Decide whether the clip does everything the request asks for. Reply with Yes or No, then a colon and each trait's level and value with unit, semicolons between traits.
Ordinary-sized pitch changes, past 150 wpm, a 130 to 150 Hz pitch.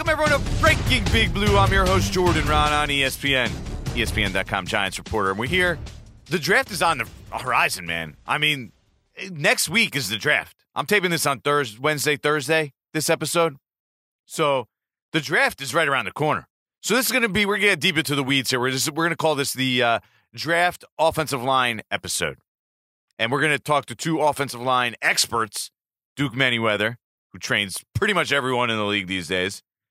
No: wide, 6.2 semitones; average, 200 wpm; medium, 140 Hz